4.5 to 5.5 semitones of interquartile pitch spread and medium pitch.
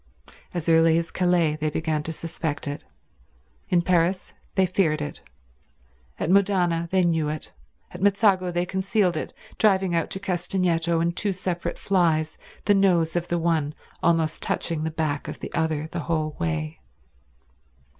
No: narrow, 2.5 semitones; medium, 170 Hz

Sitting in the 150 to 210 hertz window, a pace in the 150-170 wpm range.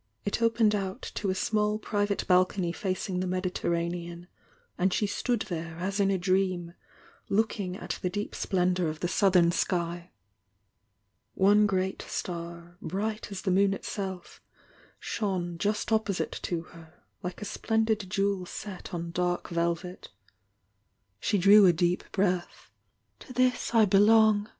No: high, 190 Hz; average, 140 wpm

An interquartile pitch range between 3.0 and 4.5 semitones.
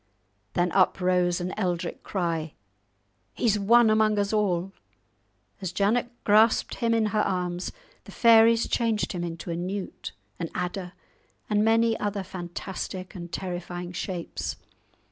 Yes: average, 3.4 semitones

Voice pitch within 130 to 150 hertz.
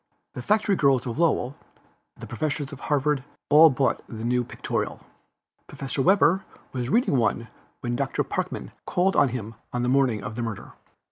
Yes: low, 135 Hz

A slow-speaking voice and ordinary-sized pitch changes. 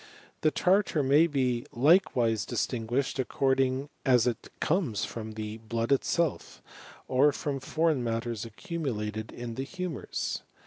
Yes: slow, 105 wpm; average, 4.4 semitones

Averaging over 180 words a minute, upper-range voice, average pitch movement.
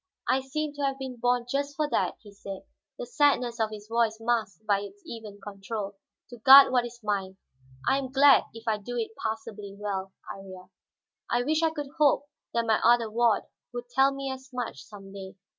Yes: average, 200 wpm; high, 235 Hz; average, 4.5 semitones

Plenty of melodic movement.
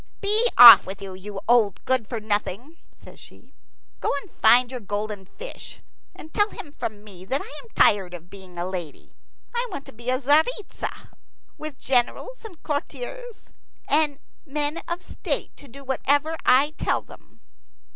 Yes: wide, 7.4 semitones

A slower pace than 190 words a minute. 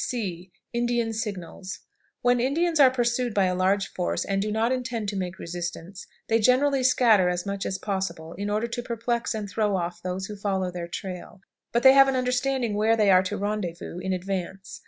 No: average, 200 wpm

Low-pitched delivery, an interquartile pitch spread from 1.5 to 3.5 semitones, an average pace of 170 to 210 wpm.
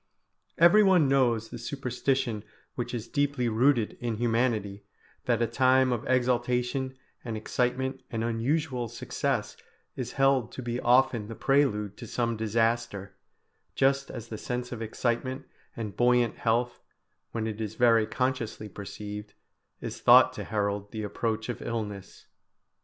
No: low, 120 Hz; average, 2.7 semitones; average, 140 wpm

